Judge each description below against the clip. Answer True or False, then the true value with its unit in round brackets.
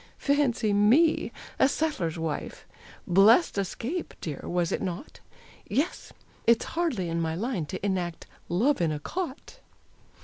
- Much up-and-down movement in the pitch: True (8.5 semitones)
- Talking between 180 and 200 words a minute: False (135 wpm)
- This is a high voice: True (205 Hz)